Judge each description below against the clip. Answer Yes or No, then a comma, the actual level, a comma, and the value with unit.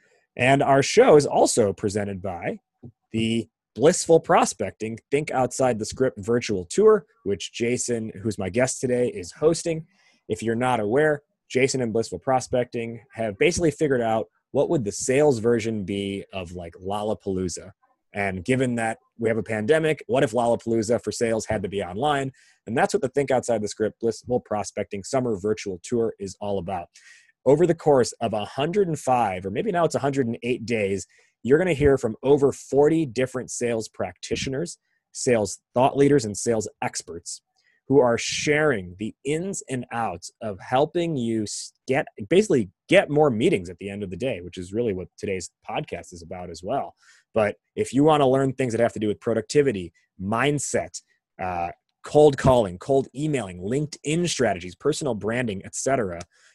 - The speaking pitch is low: Yes, low, 120 Hz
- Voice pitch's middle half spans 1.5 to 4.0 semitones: No, average, 5.2 semitones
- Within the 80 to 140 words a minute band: No, average, 170 wpm